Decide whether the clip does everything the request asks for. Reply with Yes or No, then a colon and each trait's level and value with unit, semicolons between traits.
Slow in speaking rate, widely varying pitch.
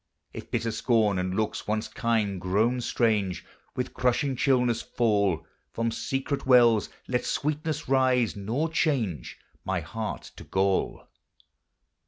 No: slow, 125 wpm; average, 4.0 semitones